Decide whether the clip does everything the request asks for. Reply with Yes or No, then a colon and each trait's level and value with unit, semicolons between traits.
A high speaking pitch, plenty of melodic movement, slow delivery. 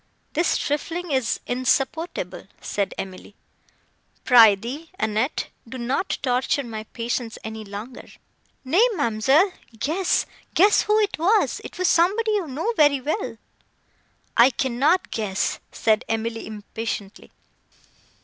Yes: very high, 255 Hz; wide, 7.0 semitones; slow, 110 wpm